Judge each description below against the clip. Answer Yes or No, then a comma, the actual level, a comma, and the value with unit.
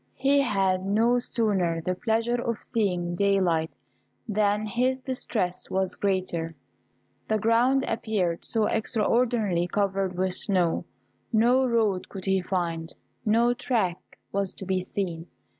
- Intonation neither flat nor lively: Yes, average, 4.0 semitones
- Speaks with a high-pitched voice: Yes, high, 200 Hz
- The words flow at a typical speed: No, slow, 125 wpm